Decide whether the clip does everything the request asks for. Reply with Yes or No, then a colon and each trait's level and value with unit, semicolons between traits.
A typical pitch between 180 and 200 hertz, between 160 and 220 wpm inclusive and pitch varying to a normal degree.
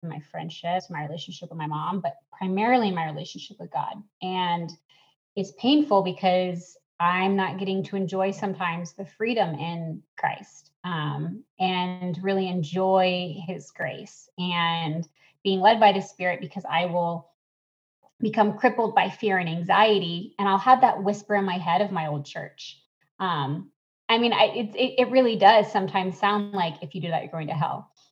Yes: medium, 185 Hz; average, 170 wpm; average, 3.1 semitones